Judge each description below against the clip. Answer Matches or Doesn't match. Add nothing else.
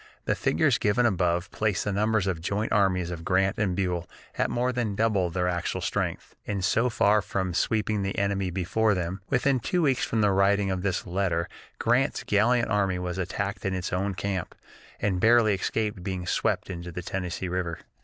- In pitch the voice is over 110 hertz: Doesn't match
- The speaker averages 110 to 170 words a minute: Doesn't match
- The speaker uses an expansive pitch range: Doesn't match